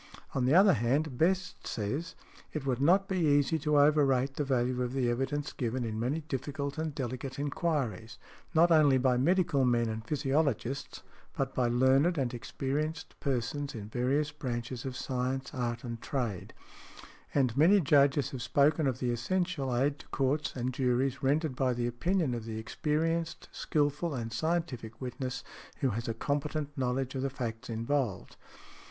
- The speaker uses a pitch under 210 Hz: Yes, low, 135 Hz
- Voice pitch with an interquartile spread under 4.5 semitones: Yes, average, 3.4 semitones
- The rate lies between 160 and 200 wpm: Yes, average, 165 wpm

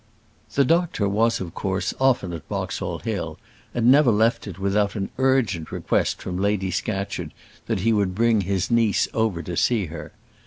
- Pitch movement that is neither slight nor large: Yes, average, 3.6 semitones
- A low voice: Yes, low, 105 Hz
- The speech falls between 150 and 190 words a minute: Yes, average, 170 wpm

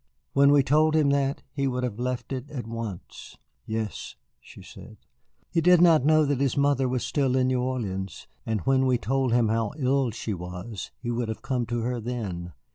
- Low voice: Yes, low, 125 Hz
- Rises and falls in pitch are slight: No, average, 3.5 semitones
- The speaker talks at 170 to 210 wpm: Yes, average, 200 wpm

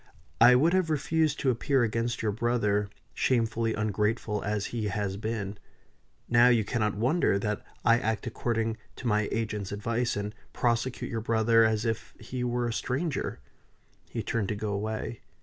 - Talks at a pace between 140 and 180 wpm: Yes, average, 165 wpm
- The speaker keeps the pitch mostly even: Yes, narrow, 2.3 semitones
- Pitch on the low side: Yes, low, 115 Hz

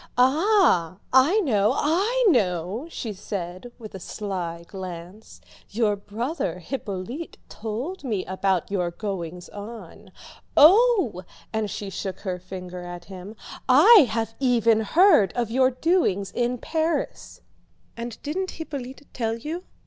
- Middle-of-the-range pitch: No, high, 220 Hz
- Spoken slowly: Yes, slow, 125 wpm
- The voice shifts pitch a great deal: Yes, wide, 7.2 semitones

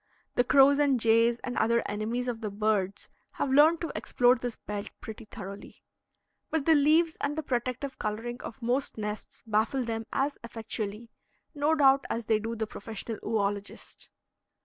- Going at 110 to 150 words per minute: No, average, 165 wpm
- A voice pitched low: No, high, 235 Hz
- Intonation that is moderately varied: Yes, average, 3.9 semitones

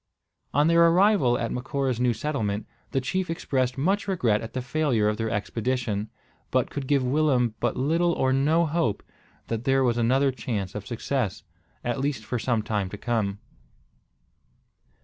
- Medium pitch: No, low, 125 Hz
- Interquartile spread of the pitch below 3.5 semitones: No, average, 4.3 semitones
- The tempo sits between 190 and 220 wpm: No, average, 165 wpm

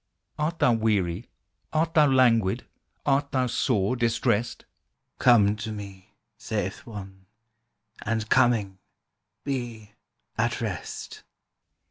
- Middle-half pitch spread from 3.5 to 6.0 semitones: Yes, average, 4.0 semitones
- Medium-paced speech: No, slow, 100 wpm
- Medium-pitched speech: No, low, 115 Hz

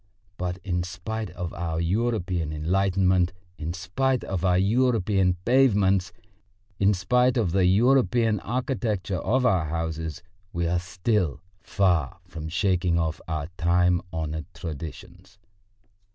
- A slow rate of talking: Yes, slow, 125 wpm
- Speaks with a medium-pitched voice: No, very low, 90 Hz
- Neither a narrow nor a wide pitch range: Yes, average, 3.8 semitones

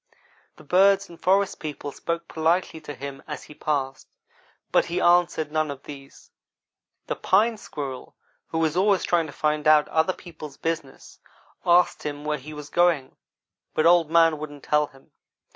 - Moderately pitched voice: Yes, medium, 155 Hz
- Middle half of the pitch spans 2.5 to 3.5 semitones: Yes, average, 2.8 semitones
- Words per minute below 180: Yes, average, 165 wpm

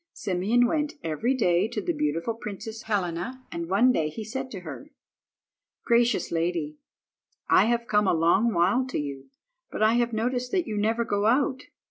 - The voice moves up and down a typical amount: No, wide, 5.7 semitones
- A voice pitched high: Yes, high, 215 Hz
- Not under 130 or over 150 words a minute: No, average, 175 wpm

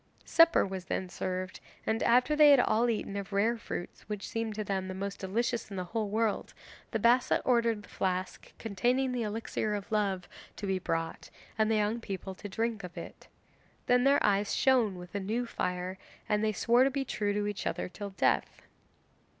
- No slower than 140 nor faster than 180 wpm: No, average, 200 wpm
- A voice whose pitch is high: Yes, high, 210 Hz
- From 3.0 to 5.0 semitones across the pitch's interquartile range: Yes, average, 3.4 semitones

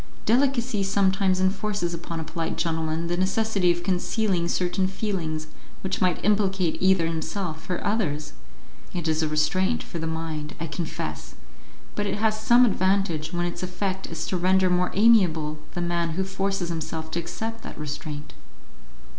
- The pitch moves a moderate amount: Yes, average, 3.2 semitones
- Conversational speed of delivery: Yes, average, 160 wpm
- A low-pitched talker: No, medium, 180 Hz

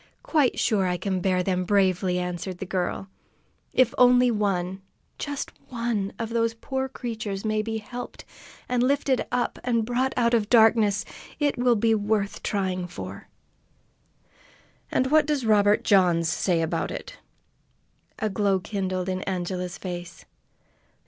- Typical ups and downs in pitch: Yes, average, 4.5 semitones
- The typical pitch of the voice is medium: No, high, 210 Hz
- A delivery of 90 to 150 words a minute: Yes, average, 140 wpm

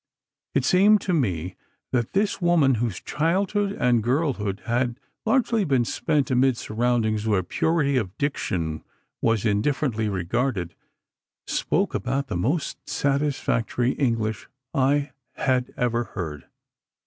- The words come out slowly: Yes, slow, 120 wpm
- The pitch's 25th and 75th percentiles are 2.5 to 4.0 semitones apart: No, average, 5.1 semitones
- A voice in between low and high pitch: No, low, 125 Hz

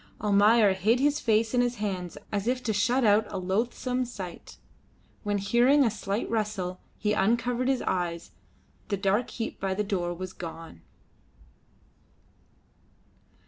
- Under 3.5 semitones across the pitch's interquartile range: No, average, 3.8 semitones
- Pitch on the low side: No, high, 210 Hz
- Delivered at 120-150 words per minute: Yes, average, 140 wpm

